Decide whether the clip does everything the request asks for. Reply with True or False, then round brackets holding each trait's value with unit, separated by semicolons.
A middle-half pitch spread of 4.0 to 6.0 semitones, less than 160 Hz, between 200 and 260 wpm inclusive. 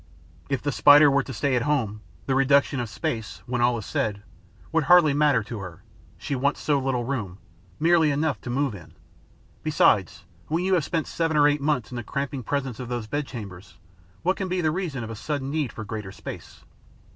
True (4.4 semitones; 135 Hz; 205 wpm)